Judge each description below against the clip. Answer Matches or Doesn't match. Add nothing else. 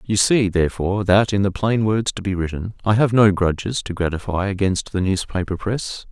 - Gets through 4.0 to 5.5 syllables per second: Matches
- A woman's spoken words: Doesn't match